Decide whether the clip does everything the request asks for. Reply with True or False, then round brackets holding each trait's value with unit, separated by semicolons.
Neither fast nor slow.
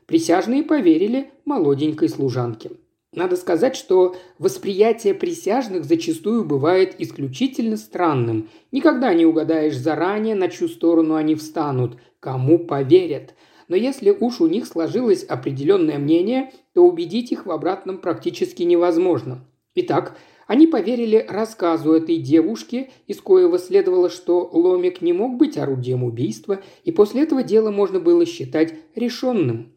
True (125 wpm)